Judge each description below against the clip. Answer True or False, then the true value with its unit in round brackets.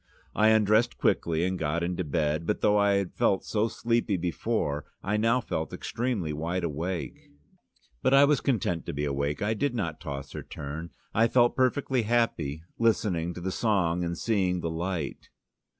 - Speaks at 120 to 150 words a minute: False (180 wpm)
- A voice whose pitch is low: True (95 Hz)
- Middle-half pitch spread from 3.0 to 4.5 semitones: False (5.5 semitones)